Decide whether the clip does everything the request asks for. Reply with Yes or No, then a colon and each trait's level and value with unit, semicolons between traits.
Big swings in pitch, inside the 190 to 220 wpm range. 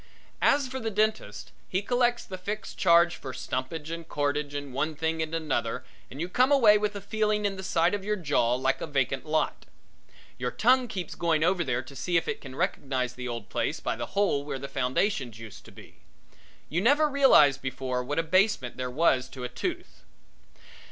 Yes: wide, 7.5 semitones; fast, 205 wpm